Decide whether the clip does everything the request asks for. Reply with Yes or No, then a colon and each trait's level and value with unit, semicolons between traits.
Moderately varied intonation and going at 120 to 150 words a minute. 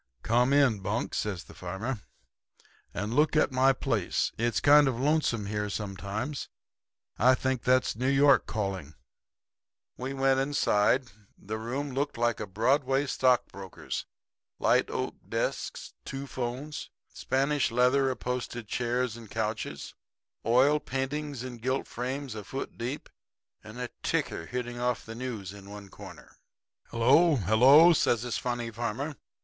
Yes: average, 3.6 semitones; average, 140 wpm